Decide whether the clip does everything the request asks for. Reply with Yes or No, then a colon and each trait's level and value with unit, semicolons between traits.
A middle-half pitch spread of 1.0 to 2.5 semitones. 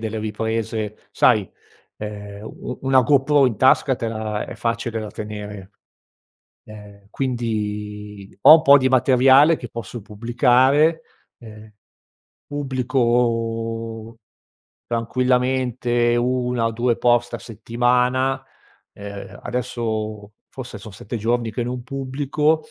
No: average, 2.9 semitones